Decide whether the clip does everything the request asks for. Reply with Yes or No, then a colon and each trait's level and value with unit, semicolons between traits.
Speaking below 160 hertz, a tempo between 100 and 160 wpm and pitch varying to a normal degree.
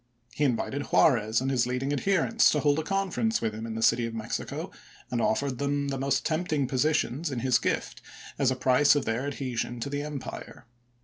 No: low, 135 Hz; average, 200 wpm; average, 3.1 semitones